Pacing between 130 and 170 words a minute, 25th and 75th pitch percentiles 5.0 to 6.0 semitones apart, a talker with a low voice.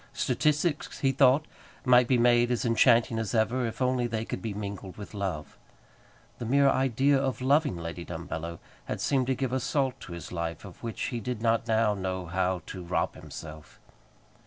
No: average, 185 wpm; wide, 5.5 semitones; low, 115 Hz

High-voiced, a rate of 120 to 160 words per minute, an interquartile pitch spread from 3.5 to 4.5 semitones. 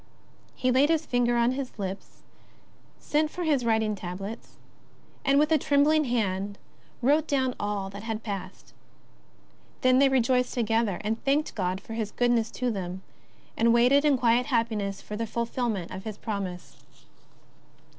Yes: high, 235 Hz; average, 155 wpm; average, 4.2 semitones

